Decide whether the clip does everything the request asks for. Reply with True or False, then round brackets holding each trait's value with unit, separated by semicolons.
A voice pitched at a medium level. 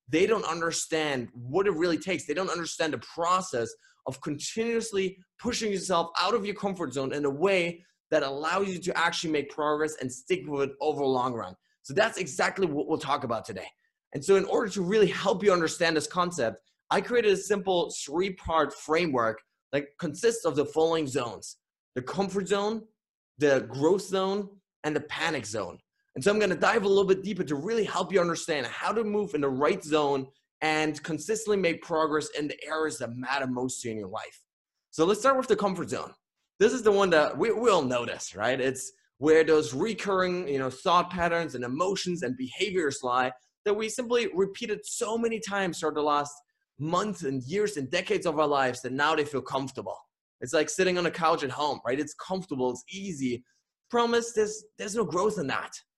True (170 Hz)